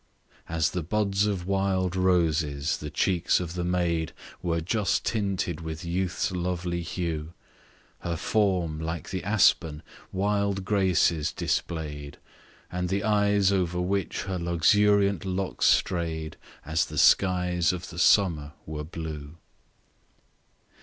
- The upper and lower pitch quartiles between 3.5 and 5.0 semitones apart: No, average, 2.9 semitones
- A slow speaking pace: Yes, slow, 125 wpm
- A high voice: No, very low, 90 Hz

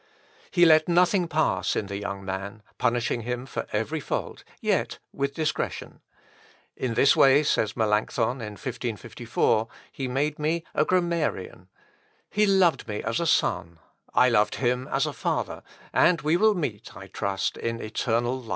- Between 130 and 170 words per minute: Yes, average, 160 wpm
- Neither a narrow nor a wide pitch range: No, wide, 6.3 semitones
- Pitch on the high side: No, low, 125 Hz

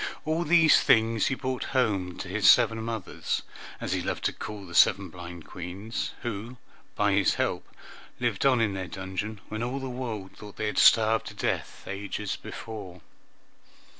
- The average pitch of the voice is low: Yes, low, 110 Hz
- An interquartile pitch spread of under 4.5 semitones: Yes, average, 3.7 semitones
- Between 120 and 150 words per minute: No, average, 170 wpm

